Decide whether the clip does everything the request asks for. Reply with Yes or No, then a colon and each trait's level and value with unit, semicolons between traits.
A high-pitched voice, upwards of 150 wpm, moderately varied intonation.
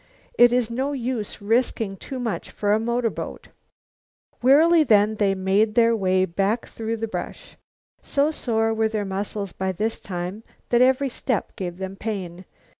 Yes: high, 220 Hz; average, 160 wpm; average, 3.7 semitones